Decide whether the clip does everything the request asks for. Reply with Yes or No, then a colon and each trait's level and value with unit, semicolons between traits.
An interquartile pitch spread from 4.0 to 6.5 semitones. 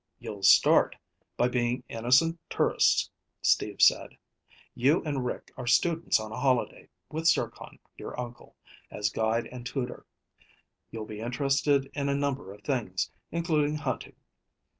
No: average, 3.6 semitones